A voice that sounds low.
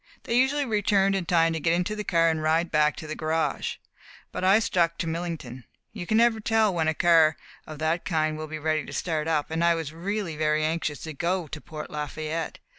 No: medium, 165 Hz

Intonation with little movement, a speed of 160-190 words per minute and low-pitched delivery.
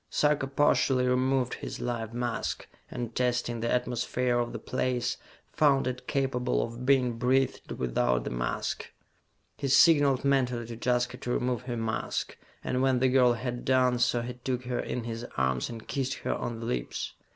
Yes: narrow, 1.6 semitones; average, 175 wpm; low, 125 Hz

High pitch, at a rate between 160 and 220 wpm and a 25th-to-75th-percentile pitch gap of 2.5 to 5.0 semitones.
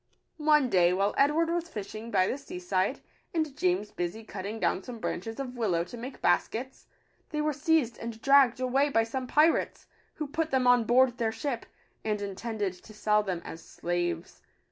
No: high, 230 Hz; average, 185 wpm; wide, 5.6 semitones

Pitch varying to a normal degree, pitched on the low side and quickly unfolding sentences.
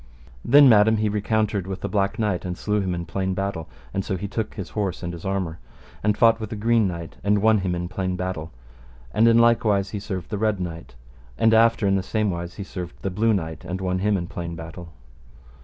Yes: average, 3.3 semitones; very low, 95 Hz; fast, 235 wpm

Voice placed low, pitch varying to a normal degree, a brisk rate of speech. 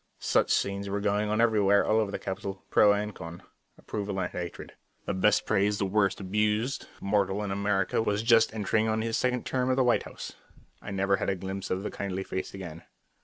No: low, 100 Hz; narrow, 1.8 semitones; fast, 215 wpm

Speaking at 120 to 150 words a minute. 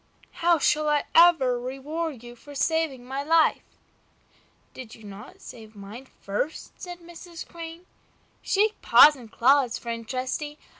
Yes: average, 140 wpm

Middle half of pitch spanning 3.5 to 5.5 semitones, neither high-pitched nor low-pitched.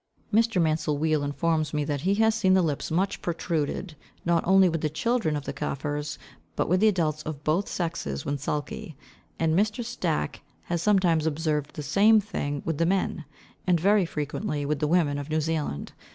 Yes: average, 4.0 semitones; medium, 160 Hz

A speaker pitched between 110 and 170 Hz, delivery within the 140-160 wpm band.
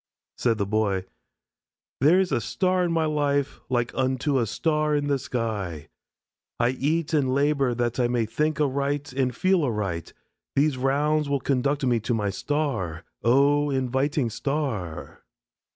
Yes: low, 135 Hz; average, 150 wpm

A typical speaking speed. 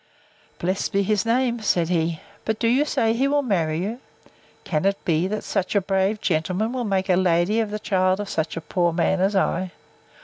No: fast, 210 wpm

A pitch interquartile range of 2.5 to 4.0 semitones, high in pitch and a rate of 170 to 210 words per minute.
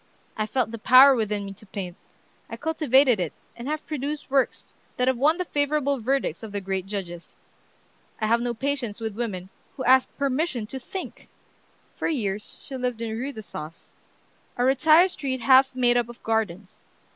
No: average, 4.4 semitones; high, 245 Hz; average, 180 wpm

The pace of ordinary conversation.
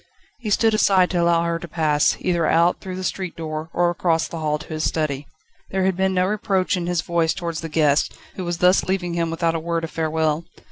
No: fast, 235 wpm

